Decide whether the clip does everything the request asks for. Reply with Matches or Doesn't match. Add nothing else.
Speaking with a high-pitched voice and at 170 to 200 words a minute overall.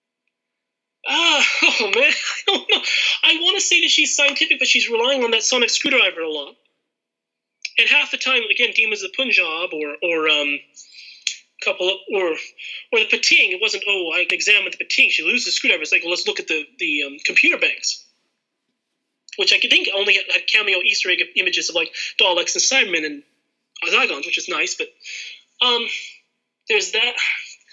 Matches